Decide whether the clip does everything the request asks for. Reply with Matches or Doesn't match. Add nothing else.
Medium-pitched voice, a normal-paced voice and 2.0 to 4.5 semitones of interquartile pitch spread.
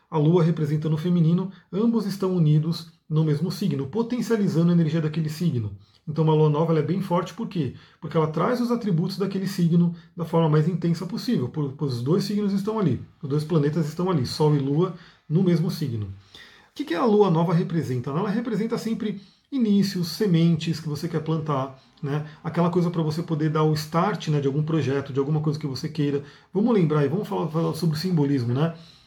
Doesn't match